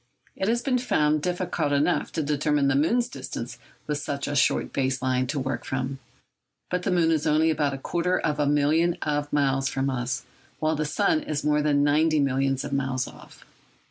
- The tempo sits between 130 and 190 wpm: No, average, 200 wpm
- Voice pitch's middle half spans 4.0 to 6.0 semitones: No, average, 2.7 semitones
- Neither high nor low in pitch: Yes, medium, 145 Hz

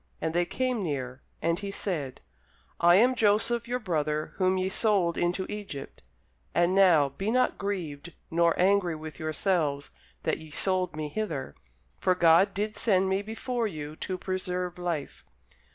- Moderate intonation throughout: Yes, average, 4.2 semitones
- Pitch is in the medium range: Yes, medium, 180 Hz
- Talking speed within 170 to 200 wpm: No, average, 155 wpm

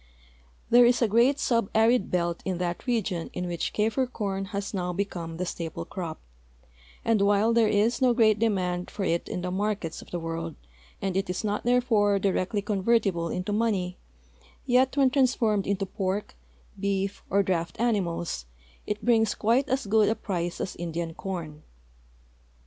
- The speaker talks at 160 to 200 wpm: Yes, average, 165 wpm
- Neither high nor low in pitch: No, high, 200 Hz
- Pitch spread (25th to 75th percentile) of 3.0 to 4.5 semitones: Yes, average, 4.0 semitones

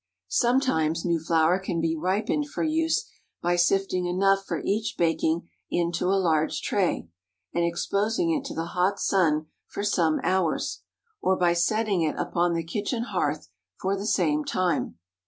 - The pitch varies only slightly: No, average, 3.3 semitones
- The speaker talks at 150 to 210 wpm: Yes, average, 155 wpm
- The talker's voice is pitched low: No, medium, 180 Hz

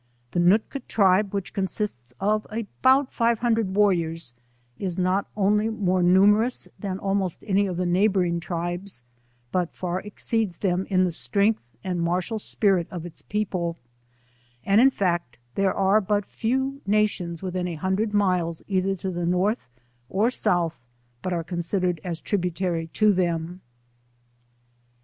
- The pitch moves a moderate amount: Yes, average, 3.0 semitones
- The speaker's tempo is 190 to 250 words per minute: No, average, 145 wpm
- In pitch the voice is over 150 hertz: Yes, high, 190 Hz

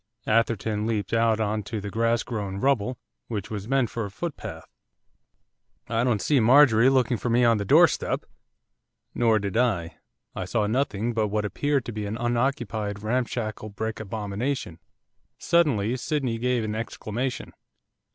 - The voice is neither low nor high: No, low, 115 Hz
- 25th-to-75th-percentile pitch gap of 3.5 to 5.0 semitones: No, average, 2.7 semitones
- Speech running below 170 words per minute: Yes, average, 150 wpm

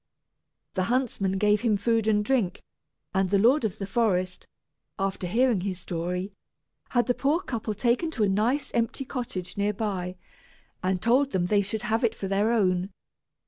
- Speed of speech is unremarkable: Yes, average, 175 wpm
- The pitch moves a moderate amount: Yes, average, 3.8 semitones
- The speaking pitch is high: Yes, high, 210 Hz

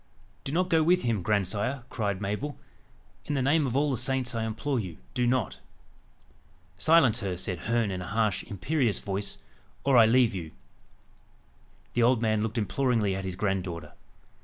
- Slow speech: No, average, 170 wpm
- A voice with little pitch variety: No, average, 4.9 semitones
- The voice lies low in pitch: Yes, low, 115 Hz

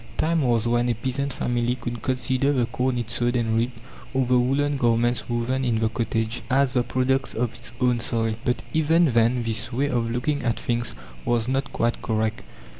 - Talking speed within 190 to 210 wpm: Yes, average, 195 wpm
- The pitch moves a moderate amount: No, narrow, 2.0 semitones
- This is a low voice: Yes, low, 120 Hz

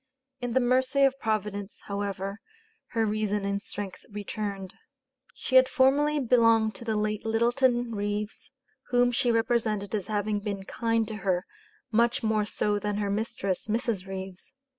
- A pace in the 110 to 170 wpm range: Yes, average, 150 wpm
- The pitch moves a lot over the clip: No, average, 2.7 semitones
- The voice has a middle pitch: No, high, 215 Hz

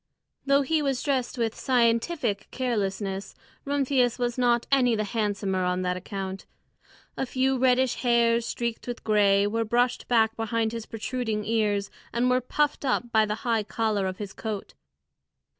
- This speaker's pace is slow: No, average, 160 wpm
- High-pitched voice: Yes, high, 230 Hz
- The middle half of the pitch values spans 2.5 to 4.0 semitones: Yes, average, 3.1 semitones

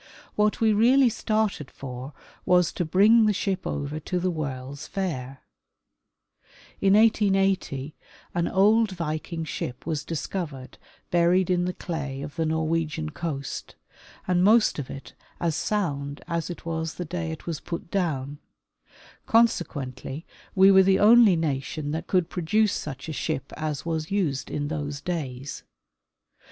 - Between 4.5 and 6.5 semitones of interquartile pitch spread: Yes, average, 4.8 semitones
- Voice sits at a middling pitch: Yes, medium, 165 Hz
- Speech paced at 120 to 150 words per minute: Yes, average, 145 wpm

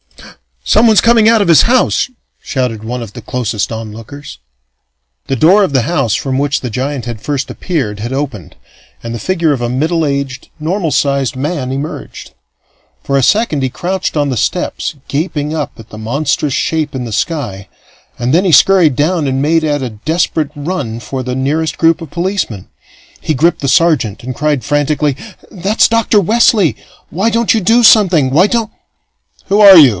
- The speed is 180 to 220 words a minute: Yes, average, 185 wpm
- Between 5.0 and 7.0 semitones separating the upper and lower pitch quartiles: Yes, wide, 5.5 semitones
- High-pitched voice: No, medium, 145 Hz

